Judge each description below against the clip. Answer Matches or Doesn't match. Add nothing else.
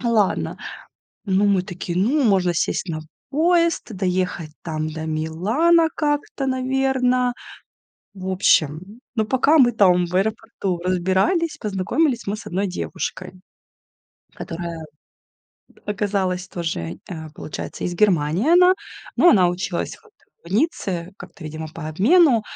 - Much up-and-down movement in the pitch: Matches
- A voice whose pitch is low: Doesn't match